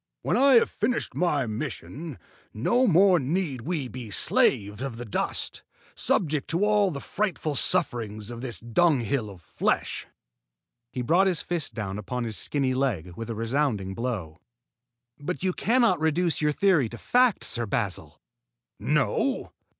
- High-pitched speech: No, low, 135 Hz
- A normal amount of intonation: No, wide, 7.6 semitones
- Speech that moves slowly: No, average, 150 wpm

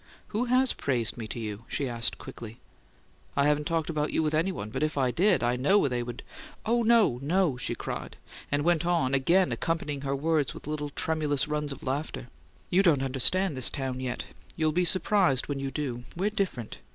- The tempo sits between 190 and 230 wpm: Yes, average, 200 wpm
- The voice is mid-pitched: Yes, medium, 150 Hz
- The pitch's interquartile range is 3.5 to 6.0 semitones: Yes, average, 5.0 semitones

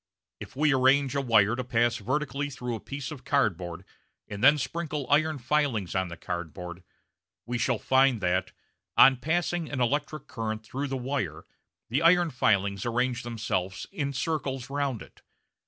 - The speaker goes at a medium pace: Yes, average, 160 wpm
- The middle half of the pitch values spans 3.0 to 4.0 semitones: No, average, 4.6 semitones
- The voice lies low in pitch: Yes, low, 130 Hz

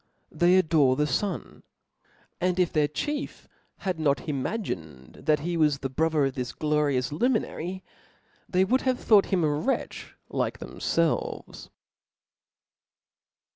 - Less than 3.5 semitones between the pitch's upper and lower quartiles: No, average, 4.5 semitones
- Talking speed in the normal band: No, slow, 130 wpm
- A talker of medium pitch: Yes, medium, 160 Hz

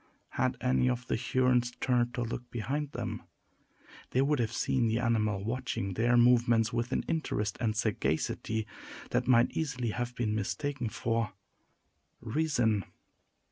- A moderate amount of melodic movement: No, narrow, 2.3 semitones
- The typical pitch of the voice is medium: No, low, 120 Hz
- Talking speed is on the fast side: No, average, 140 wpm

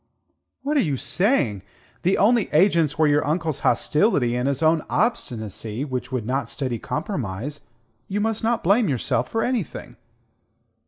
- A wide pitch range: Yes, wide, 8.4 semitones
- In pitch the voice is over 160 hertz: No, medium, 150 Hz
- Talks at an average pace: Yes, average, 150 wpm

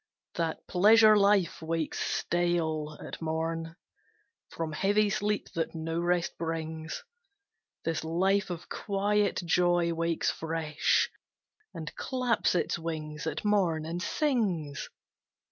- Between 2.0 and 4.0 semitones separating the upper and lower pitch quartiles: Yes, average, 3.5 semitones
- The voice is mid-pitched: Yes, medium, 170 Hz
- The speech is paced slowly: Yes, slow, 110 wpm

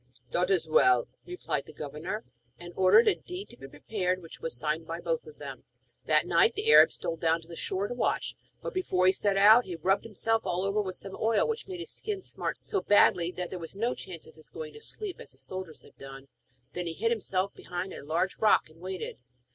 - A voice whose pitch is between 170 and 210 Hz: Yes, high, 190 Hz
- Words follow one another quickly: Yes, fast, 235 wpm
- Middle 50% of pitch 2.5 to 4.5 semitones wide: No, average, 5.1 semitones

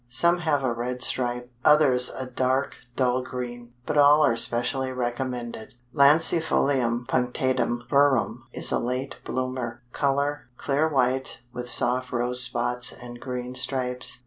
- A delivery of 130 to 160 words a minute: Yes, slow, 135 wpm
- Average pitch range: No, narrow, 1.9 semitones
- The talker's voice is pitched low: Yes, low, 125 Hz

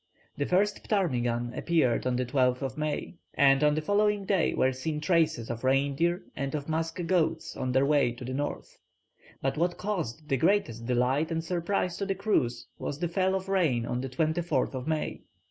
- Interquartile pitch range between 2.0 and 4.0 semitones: No, average, 5.1 semitones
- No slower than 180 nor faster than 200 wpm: Yes, average, 185 wpm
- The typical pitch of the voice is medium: Yes, medium, 150 Hz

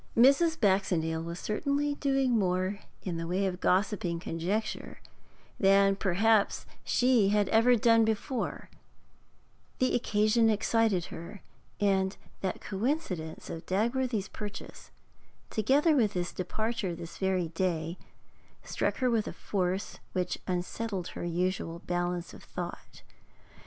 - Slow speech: Yes, slow, 120 wpm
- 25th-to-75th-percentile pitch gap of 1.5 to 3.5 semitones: No, average, 4.1 semitones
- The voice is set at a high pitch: Yes, high, 200 Hz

